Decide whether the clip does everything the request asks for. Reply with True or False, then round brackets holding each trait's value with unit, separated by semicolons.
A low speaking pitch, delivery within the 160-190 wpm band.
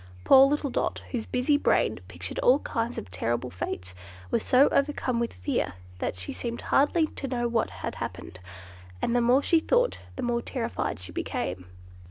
False (240 Hz; 180 wpm)